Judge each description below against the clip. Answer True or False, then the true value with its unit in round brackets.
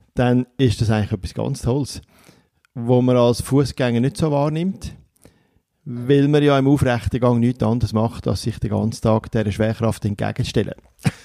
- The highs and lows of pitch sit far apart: False (2.9 semitones)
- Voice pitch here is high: False (120 Hz)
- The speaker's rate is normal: True (165 wpm)